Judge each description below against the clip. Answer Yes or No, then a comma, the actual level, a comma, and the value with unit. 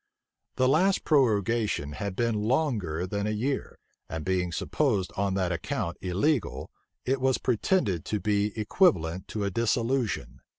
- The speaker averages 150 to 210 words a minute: No, average, 140 wpm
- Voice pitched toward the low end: Yes, low, 105 Hz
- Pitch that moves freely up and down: Yes, wide, 5.7 semitones